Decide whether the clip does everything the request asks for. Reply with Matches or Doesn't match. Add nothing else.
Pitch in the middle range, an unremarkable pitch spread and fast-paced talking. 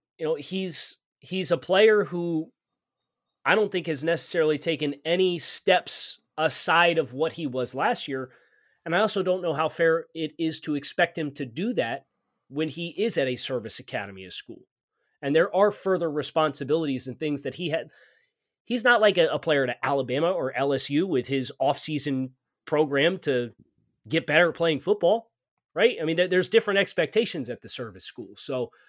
Doesn't match